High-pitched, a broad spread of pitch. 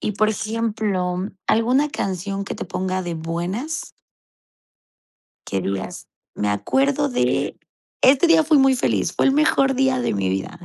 Yes: high, 215 Hz; wide, 7.1 semitones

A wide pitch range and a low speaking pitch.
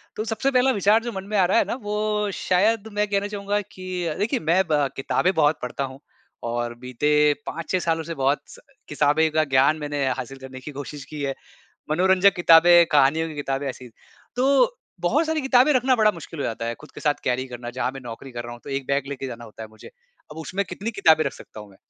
No: wide, 7.0 semitones; medium, 155 Hz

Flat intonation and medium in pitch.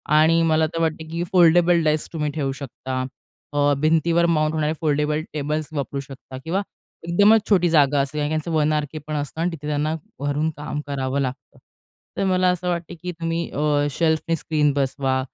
Yes: narrow, 2.3 semitones; medium, 155 Hz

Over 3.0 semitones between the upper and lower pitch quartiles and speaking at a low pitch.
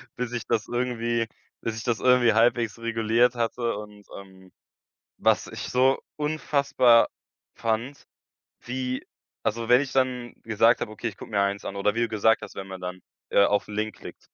No: average, 2.7 semitones; low, 115 Hz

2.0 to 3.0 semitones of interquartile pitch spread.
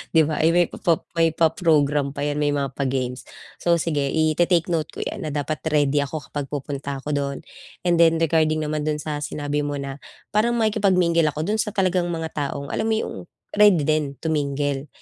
Yes: average, 2.7 semitones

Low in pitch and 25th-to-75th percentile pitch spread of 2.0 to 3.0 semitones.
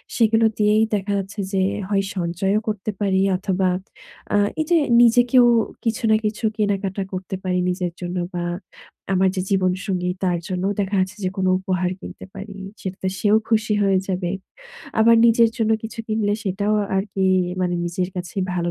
No: high, 195 Hz; narrow, 2.6 semitones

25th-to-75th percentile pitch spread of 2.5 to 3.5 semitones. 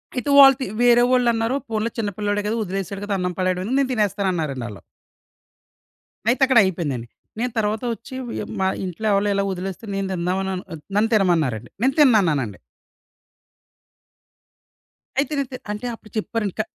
No: average, 4.3 semitones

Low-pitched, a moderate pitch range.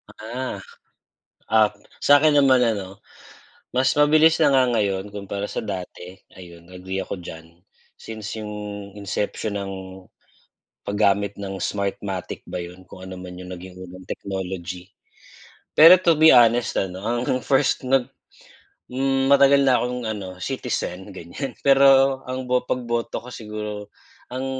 No: low, 105 Hz; wide, 5.7 semitones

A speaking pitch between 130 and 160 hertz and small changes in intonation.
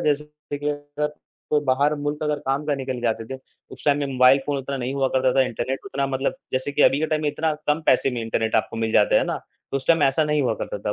Yes: medium, 140 Hz; narrow, 2.3 semitones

